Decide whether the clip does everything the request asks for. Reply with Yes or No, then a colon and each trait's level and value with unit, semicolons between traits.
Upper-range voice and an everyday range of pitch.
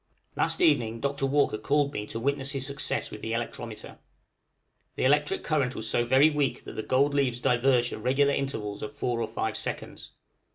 No: low, 130 Hz; average, 3.4 semitones